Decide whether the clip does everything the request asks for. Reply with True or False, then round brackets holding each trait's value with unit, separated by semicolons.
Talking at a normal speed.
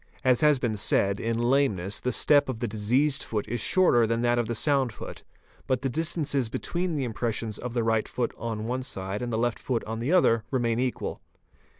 False (215 wpm)